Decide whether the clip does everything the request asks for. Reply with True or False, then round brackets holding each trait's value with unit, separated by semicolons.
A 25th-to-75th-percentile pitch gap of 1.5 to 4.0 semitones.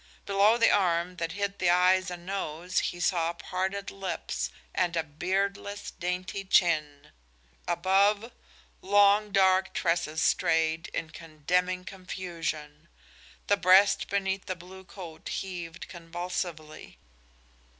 True (2.5 semitones)